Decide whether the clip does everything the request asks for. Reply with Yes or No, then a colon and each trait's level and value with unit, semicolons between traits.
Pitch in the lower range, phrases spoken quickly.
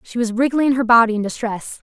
No: high, 235 Hz; fast, 220 wpm